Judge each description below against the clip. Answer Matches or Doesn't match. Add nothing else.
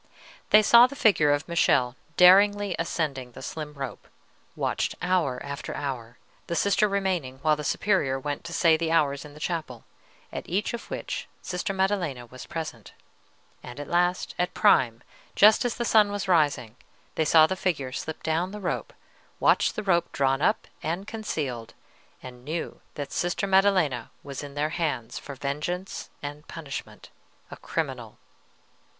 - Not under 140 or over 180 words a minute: Matches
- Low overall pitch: Doesn't match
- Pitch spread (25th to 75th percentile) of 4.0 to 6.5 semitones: Matches